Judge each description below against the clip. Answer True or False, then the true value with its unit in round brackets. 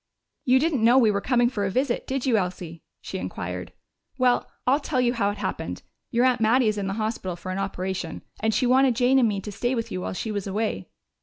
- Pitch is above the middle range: True (225 Hz)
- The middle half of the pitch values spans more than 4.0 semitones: True (4.4 semitones)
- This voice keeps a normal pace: False (240 wpm)